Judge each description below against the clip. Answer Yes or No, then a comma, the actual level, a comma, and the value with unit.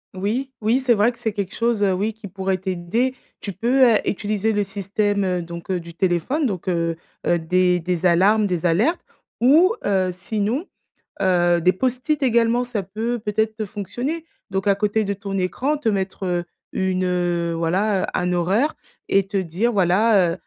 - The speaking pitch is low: No, high, 200 Hz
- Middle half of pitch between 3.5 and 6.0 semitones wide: Yes, average, 3.9 semitones